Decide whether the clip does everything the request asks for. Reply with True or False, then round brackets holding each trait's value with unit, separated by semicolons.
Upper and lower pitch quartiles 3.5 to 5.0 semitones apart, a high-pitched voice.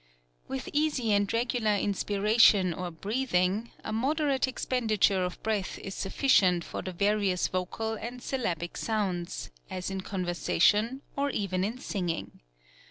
True (4.2 semitones; 205 Hz)